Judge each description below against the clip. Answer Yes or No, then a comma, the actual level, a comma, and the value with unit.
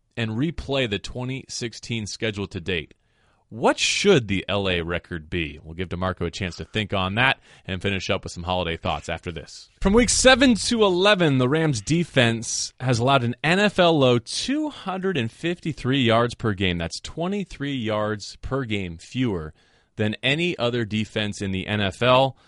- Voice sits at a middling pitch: No, low, 115 Hz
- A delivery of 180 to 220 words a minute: No, average, 165 wpm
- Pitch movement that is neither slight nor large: No, wide, 6.6 semitones